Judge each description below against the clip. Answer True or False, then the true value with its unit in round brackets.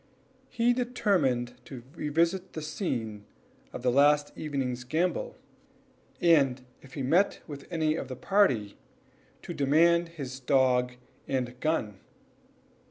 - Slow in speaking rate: True (120 wpm)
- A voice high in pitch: False (145 Hz)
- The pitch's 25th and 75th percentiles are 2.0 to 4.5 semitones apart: False (5.2 semitones)